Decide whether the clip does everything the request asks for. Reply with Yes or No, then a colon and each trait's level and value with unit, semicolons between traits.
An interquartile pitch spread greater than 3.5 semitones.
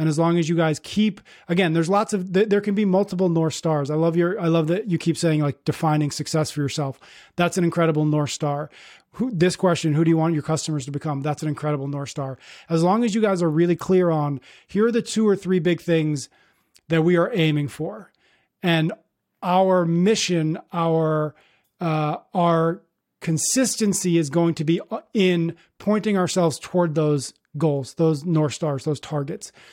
No: average, 2.9 semitones